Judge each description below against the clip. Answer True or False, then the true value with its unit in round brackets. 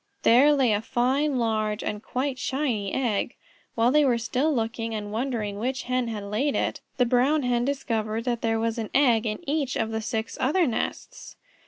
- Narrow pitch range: False (3.2 semitones)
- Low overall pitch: False (240 Hz)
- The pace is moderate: True (190 wpm)